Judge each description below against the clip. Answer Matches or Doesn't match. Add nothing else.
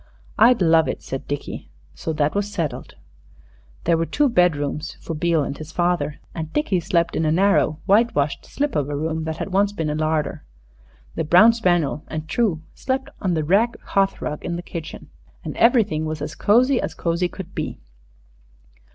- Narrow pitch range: Doesn't match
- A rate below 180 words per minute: Doesn't match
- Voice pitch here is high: Doesn't match